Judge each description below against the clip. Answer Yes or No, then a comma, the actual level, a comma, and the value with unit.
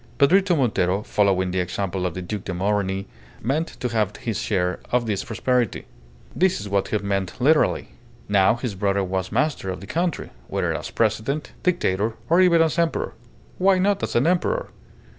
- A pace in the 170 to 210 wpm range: Yes, average, 180 wpm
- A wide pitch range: Yes, wide, 8.3 semitones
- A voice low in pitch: Yes, low, 110 Hz